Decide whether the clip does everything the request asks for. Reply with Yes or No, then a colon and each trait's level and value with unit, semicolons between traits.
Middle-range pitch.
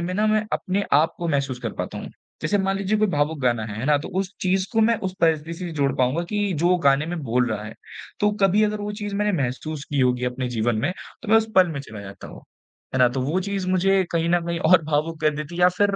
Yes: medium, 165 Hz